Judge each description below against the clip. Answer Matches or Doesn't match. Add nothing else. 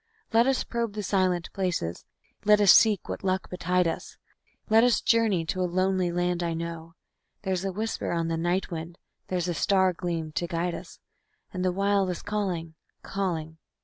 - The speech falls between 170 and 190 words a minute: Matches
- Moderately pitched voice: Matches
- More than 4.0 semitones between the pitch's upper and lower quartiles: Doesn't match